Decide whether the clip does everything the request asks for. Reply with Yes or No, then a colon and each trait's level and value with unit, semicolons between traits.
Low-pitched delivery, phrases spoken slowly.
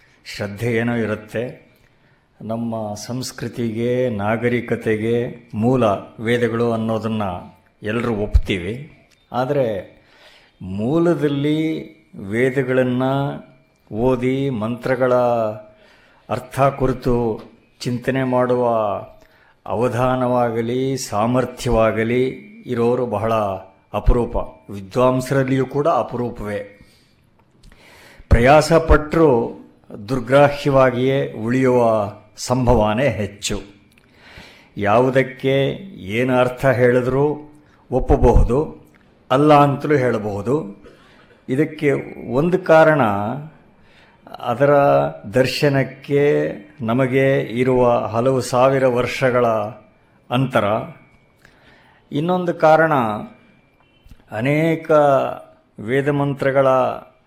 Yes: low, 125 Hz; slow, 60 wpm